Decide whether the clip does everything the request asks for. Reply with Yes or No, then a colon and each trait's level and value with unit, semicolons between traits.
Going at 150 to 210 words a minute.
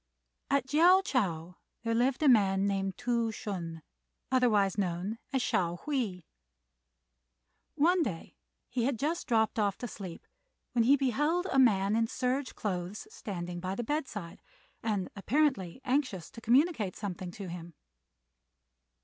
No: average, 140 wpm